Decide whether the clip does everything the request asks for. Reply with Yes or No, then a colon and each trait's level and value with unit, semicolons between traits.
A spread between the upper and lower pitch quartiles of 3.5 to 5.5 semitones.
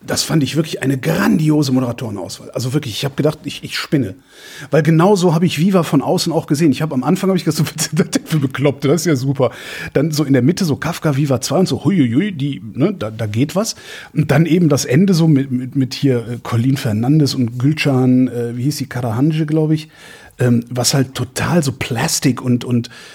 Yes: average, 4.1 semitones